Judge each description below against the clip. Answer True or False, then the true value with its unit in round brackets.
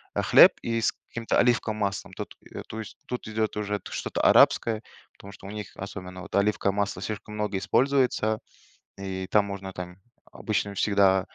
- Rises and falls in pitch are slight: True (1.9 semitones)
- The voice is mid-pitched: False (105 Hz)